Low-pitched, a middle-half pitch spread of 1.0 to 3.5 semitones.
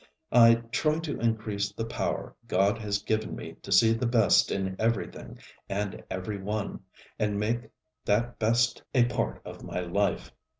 Yes: low, 110 Hz; narrow, 2.4 semitones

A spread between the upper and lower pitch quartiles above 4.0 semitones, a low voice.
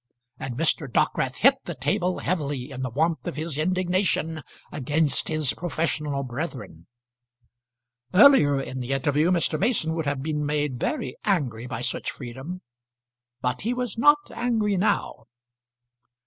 No: average, 5.3 semitones; medium, 155 Hz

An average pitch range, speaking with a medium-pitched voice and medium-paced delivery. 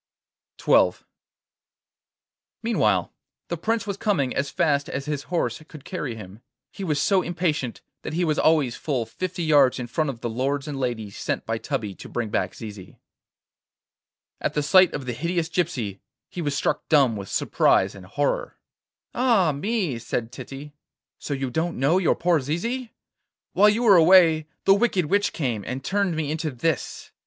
No: wide, 5.9 semitones; medium, 150 Hz; average, 170 wpm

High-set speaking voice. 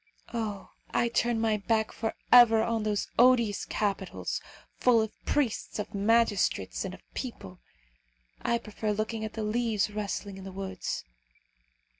Yes: high, 220 Hz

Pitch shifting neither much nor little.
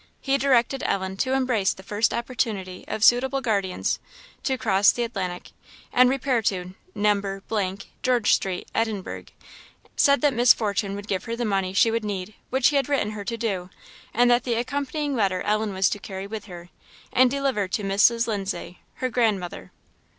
Yes: average, 4.2 semitones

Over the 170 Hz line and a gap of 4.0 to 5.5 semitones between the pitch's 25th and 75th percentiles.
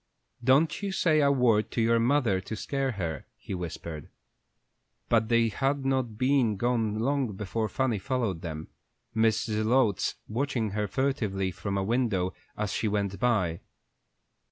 No: low, 110 Hz; average, 4.7 semitones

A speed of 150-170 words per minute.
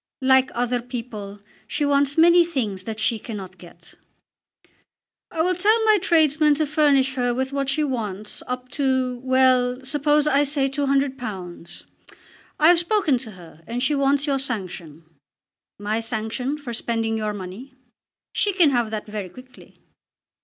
Yes: average, 155 wpm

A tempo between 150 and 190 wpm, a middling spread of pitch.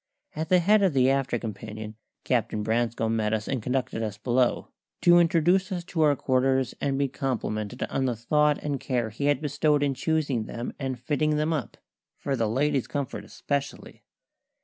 Yes: average, 180 wpm; average, 4.3 semitones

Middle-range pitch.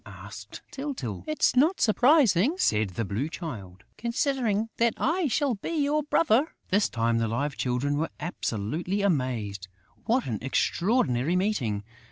Yes: medium, 180 Hz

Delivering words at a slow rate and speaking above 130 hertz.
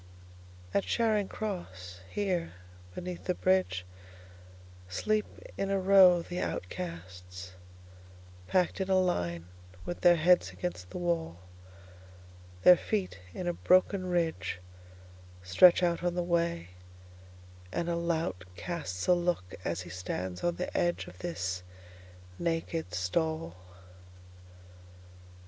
No: slow, 105 wpm; very low, 95 Hz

